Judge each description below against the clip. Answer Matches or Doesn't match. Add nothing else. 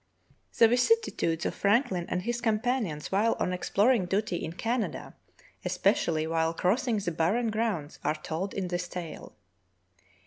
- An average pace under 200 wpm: Matches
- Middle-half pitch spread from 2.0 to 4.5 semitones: Doesn't match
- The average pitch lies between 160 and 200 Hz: Matches